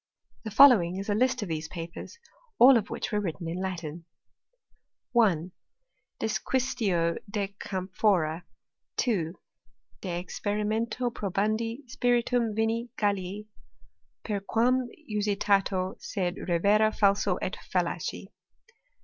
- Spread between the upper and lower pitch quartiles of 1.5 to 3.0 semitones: No, average, 3.7 semitones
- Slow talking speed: Yes, slow, 105 wpm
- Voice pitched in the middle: No, high, 205 Hz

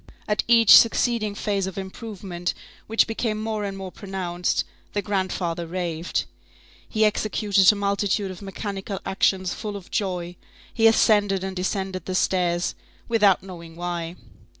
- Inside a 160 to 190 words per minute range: No, average, 140 wpm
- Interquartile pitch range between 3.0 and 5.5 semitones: No, narrow, 2.6 semitones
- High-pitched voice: Yes, high, 195 Hz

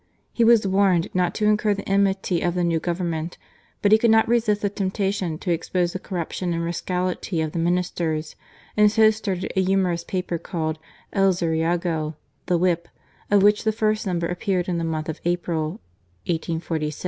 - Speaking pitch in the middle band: Yes, medium, 180 Hz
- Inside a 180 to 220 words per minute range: Yes, average, 190 wpm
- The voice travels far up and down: No, average, 3.0 semitones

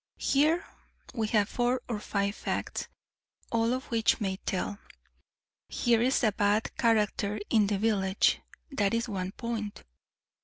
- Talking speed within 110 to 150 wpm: Yes, average, 140 wpm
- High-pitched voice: Yes, high, 215 Hz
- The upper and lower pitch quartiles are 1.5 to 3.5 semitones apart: Yes, narrow, 2.5 semitones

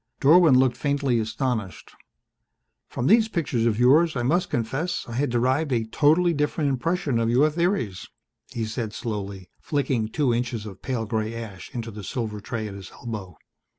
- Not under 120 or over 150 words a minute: No, average, 170 wpm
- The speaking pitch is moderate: No, low, 120 Hz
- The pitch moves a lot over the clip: No, average, 4.7 semitones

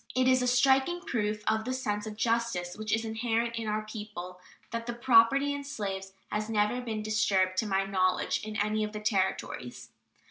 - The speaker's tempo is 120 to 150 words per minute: No, average, 190 wpm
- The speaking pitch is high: Yes, high, 215 Hz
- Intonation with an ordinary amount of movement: No, narrow, 2.3 semitones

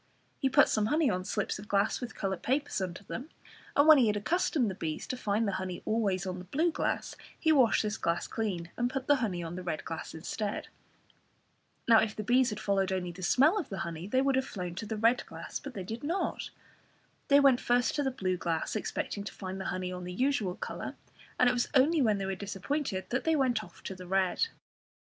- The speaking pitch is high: Yes, high, 210 Hz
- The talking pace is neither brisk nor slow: No, fast, 235 wpm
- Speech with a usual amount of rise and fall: No, wide, 5.8 semitones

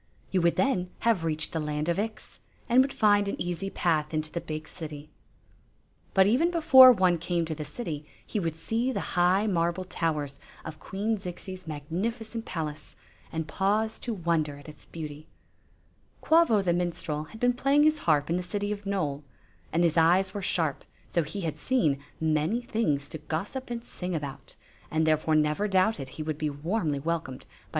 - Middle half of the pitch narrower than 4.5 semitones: No, average, 5.2 semitones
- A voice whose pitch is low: No, medium, 170 Hz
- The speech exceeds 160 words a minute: Yes, average, 190 wpm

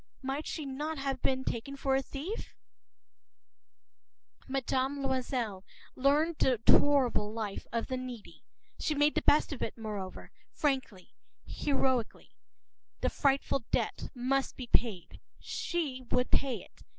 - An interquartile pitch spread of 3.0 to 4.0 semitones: No, narrow, 2.6 semitones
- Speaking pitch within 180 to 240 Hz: No, very high, 265 Hz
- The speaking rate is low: Yes, slow, 130 wpm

